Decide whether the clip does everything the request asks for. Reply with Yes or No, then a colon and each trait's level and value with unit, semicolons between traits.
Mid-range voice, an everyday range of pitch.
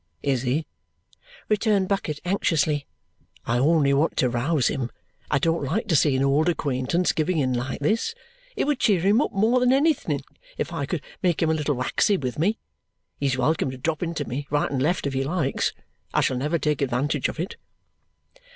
Yes: medium, 150 Hz; average, 4.7 semitones